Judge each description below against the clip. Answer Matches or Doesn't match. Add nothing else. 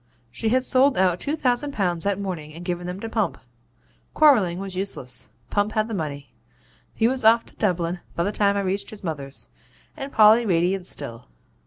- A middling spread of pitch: Matches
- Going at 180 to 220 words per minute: Matches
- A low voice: Doesn't match